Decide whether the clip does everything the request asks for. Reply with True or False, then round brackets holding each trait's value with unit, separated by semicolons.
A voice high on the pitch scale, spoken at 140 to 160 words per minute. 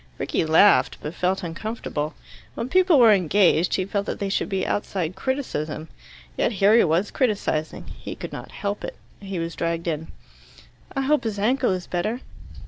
False (195 Hz; 175 wpm)